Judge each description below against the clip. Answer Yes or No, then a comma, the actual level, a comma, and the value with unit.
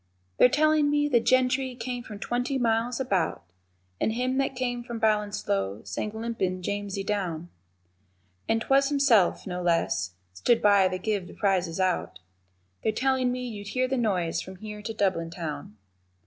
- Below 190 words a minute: Yes, average, 160 wpm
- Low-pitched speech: No, high, 215 Hz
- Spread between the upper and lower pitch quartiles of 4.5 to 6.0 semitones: Yes, average, 5.2 semitones